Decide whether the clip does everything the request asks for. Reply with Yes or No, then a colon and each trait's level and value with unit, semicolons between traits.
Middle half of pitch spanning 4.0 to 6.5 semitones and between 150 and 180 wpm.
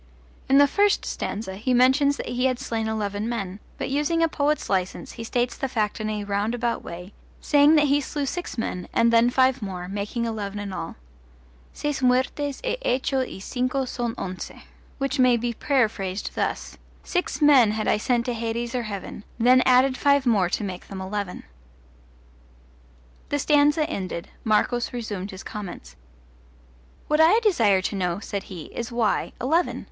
Yes: average, 4.9 semitones; average, 170 wpm